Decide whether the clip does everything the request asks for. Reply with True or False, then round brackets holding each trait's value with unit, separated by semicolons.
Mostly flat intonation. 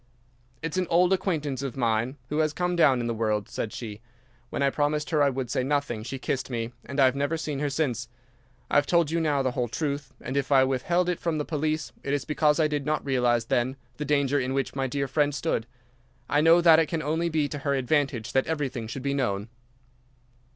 False (3.2 semitones)